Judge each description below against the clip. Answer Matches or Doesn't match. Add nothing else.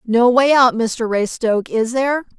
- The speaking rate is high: Doesn't match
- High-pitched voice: Matches